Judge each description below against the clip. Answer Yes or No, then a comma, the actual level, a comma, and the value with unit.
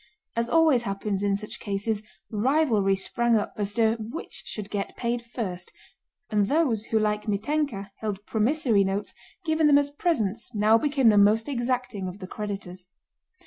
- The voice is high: Yes, high, 220 Hz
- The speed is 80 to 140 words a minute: No, average, 160 wpm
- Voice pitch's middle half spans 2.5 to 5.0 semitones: Yes, average, 3.6 semitones